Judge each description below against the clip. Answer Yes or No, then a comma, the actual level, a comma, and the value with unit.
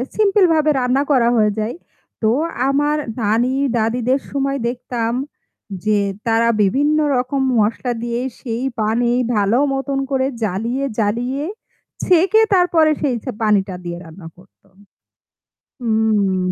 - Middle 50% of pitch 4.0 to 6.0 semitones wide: Yes, average, 4.4 semitones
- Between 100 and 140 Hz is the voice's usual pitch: No, high, 240 Hz